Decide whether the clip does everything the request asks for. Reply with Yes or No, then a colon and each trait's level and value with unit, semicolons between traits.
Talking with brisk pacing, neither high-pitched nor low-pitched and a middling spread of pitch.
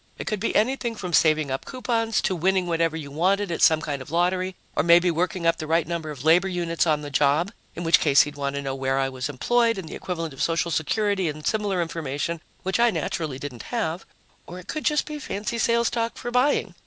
Yes: fast, 235 wpm; medium, 170 Hz; average, 4.9 semitones